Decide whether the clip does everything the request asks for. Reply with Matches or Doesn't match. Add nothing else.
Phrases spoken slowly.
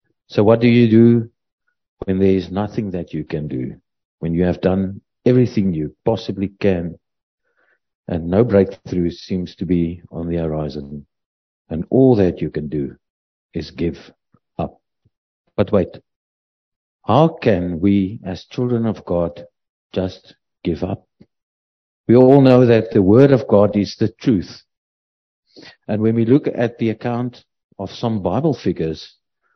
Doesn't match